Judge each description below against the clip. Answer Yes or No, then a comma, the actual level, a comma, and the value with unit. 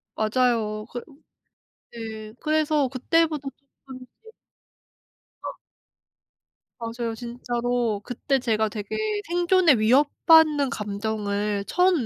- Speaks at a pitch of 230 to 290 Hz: Yes, high, 245 Hz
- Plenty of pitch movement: No, average, 4.9 semitones